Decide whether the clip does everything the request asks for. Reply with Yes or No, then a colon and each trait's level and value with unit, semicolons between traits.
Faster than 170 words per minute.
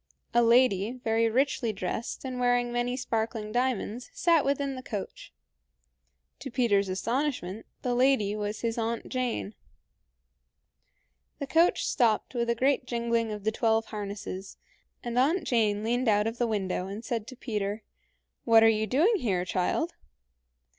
No: average, 150 wpm